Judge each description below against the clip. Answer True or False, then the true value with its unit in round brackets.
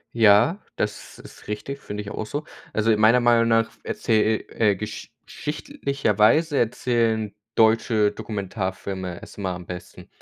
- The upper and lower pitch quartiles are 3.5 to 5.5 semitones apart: False (2.4 semitones)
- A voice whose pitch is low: True (110 Hz)